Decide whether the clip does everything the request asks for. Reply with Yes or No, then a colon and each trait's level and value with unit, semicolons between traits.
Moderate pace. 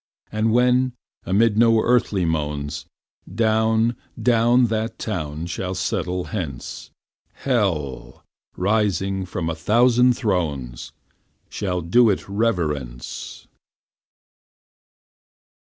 No: slow, 90 wpm